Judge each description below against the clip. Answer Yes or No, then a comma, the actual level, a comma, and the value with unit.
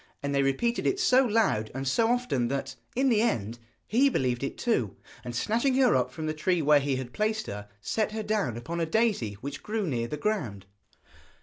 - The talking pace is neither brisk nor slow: No, fast, 210 wpm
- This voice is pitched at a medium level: Yes, medium, 155 Hz